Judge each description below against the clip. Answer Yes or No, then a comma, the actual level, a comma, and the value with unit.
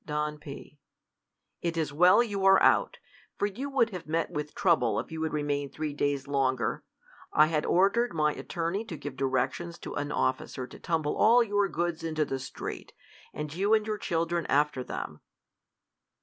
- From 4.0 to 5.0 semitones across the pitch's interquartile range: Yes, average, 4.6 semitones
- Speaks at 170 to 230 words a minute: Yes, average, 180 wpm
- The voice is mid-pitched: Yes, medium, 160 Hz